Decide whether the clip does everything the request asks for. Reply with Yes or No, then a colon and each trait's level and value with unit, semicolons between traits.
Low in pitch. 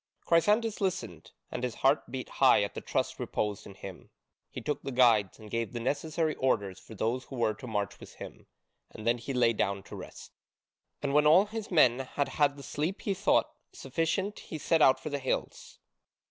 Yes: low, 130 Hz